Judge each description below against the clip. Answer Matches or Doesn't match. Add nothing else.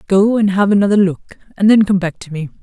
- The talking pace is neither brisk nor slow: Doesn't match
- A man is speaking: Doesn't match